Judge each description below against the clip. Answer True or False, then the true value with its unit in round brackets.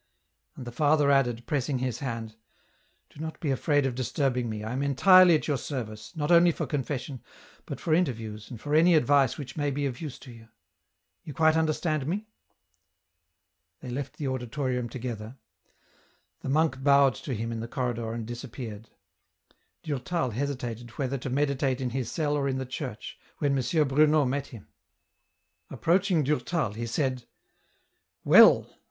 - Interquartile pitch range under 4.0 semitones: True (3.5 semitones)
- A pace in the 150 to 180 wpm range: True (170 wpm)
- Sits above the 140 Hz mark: False (135 Hz)